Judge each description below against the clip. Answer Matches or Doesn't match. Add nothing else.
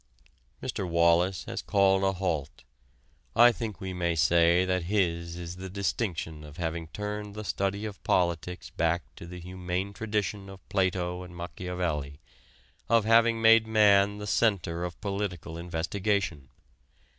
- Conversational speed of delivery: Matches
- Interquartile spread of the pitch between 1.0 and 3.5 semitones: Matches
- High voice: Doesn't match